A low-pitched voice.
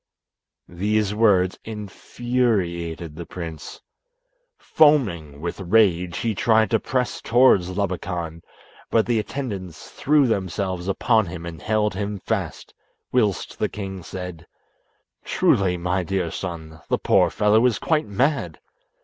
Yes: very low, 95 Hz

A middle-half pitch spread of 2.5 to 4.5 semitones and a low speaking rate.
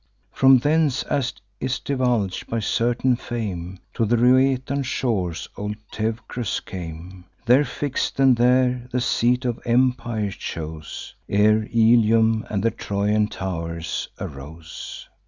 Yes: average, 4.1 semitones; slow, 120 wpm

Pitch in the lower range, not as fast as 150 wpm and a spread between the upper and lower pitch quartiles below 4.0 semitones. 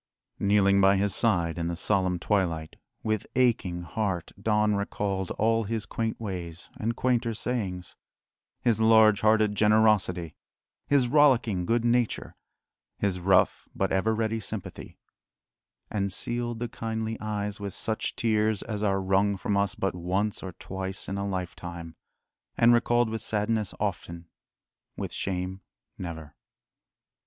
Yes: low, 100 Hz; slow, 135 wpm; average, 3.0 semitones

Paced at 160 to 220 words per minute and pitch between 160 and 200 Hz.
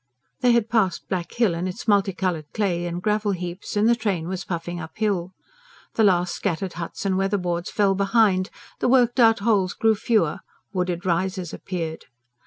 Yes: average, 170 wpm; high, 190 Hz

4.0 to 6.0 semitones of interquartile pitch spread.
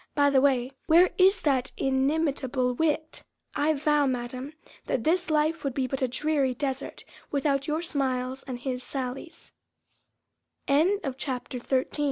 No: average, 3.0 semitones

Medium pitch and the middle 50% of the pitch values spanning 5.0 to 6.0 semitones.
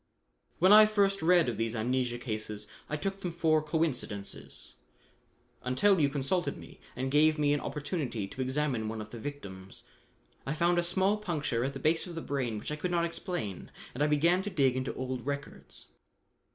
Yes: medium, 145 Hz; wide, 5.5 semitones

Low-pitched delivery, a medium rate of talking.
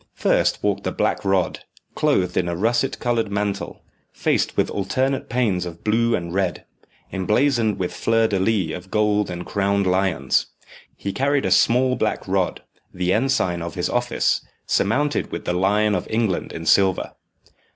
Yes: low, 100 Hz; average, 160 wpm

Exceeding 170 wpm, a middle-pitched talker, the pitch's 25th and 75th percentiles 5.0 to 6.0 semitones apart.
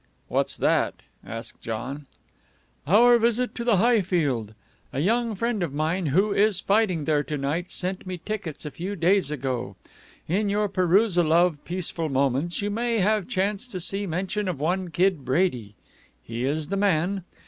No: average, 165 wpm; medium, 180 Hz; average, 5.3 semitones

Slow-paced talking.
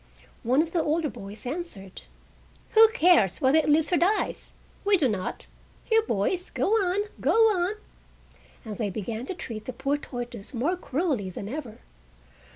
No: average, 165 wpm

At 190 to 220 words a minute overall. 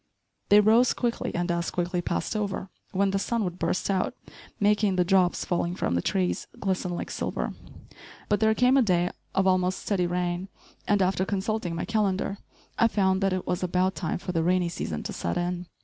Yes: average, 195 wpm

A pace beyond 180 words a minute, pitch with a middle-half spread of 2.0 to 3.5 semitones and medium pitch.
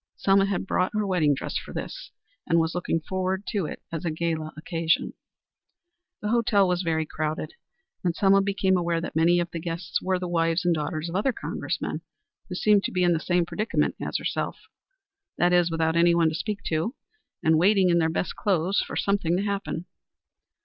Yes: average, 195 wpm; average, 2.8 semitones; medium, 175 Hz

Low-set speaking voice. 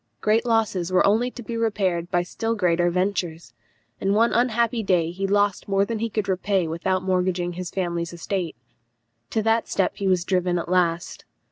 No: high, 190 Hz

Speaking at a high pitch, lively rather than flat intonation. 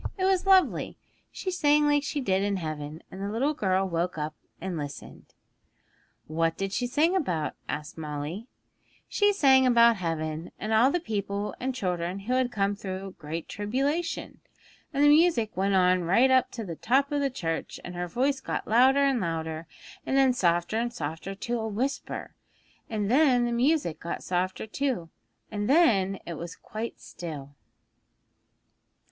Yes: high, 205 Hz; wide, 7.4 semitones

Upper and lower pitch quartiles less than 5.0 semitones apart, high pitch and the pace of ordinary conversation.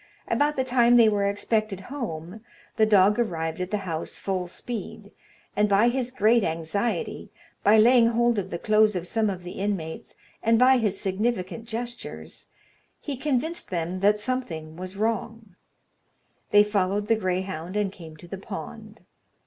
Yes: average, 4.1 semitones; high, 210 Hz; average, 160 wpm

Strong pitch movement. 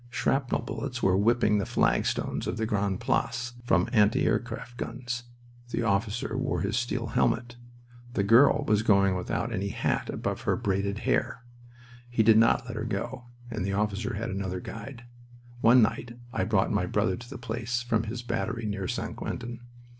No: average, 2.9 semitones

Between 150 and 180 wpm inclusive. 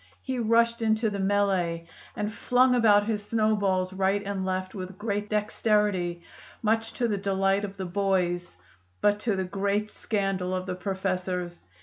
Yes: average, 155 wpm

